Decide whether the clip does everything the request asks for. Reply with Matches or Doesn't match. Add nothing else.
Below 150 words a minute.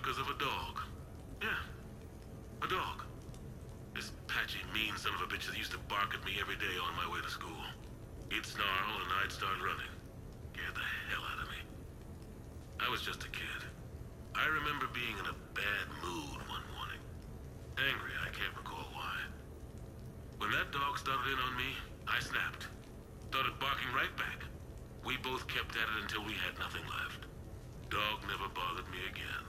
Doesn't match